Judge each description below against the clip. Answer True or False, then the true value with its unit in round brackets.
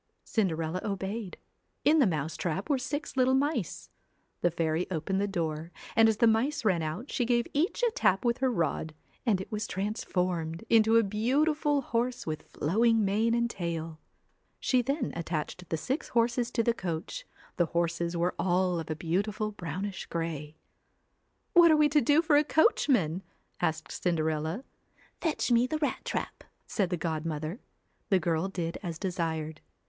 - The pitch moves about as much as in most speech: False (6.5 semitones)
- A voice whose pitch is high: True (195 Hz)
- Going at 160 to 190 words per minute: True (175 wpm)